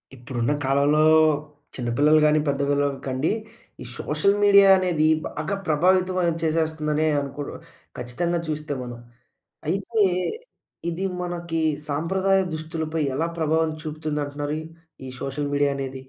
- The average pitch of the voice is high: No, medium, 155 Hz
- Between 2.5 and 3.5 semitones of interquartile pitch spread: Yes, average, 3.0 semitones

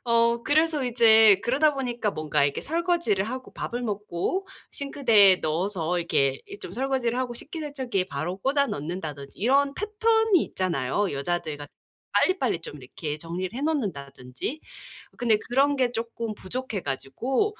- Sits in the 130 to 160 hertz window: No, high, 230 Hz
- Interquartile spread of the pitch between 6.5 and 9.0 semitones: Yes, wide, 8.1 semitones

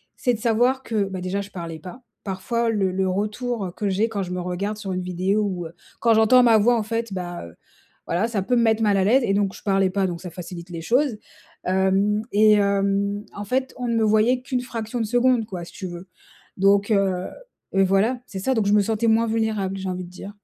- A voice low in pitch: No, high, 205 Hz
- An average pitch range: Yes, average, 3.2 semitones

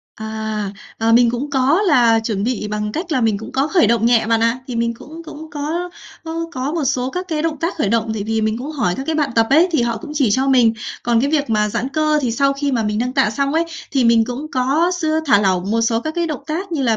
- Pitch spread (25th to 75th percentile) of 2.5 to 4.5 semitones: No, average, 5.2 semitones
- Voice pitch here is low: No, very high, 255 Hz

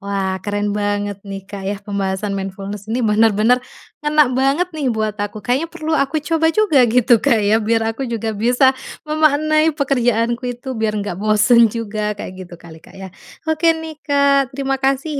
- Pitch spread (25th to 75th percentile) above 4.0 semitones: Yes, wide, 5.4 semitones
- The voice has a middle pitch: No, high, 230 Hz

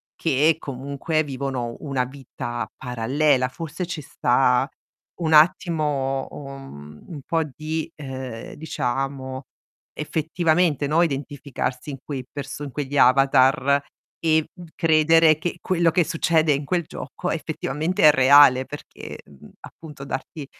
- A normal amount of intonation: Yes, average, 3.1 semitones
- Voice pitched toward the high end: No, medium, 145 Hz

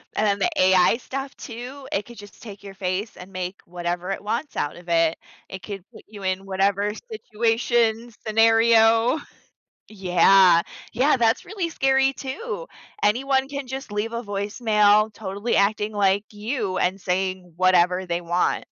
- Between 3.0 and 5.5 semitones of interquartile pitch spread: Yes, average, 3.9 semitones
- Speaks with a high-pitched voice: Yes, high, 210 Hz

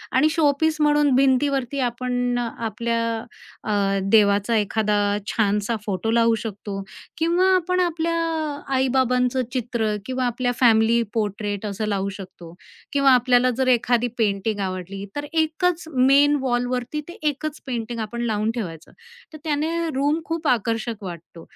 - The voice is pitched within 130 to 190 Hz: No, high, 245 Hz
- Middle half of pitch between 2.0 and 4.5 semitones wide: No, average, 4.9 semitones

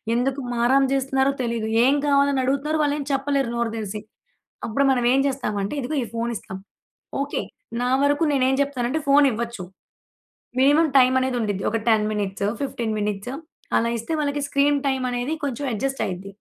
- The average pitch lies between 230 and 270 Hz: Yes, very high, 260 Hz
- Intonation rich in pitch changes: No, average, 3.6 semitones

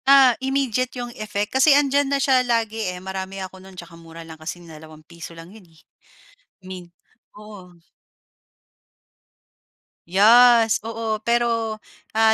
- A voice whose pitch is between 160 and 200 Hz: No, high, 215 Hz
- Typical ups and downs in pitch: Yes, average, 4.9 semitones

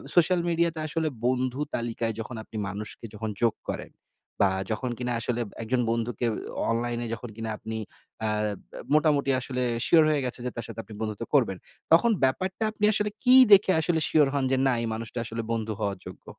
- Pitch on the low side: Yes, low, 125 Hz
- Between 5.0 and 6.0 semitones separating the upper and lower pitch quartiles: Yes, average, 5.3 semitones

